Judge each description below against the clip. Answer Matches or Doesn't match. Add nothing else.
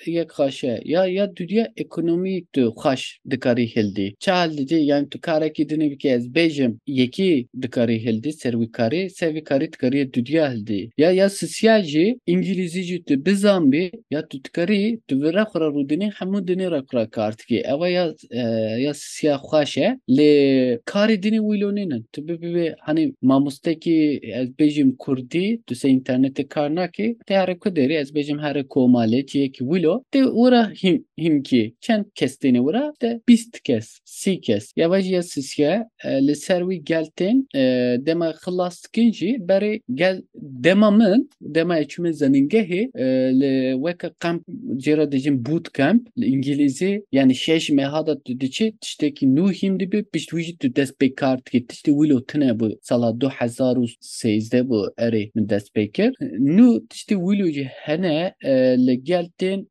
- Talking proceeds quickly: Matches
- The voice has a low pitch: Doesn't match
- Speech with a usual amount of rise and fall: Doesn't match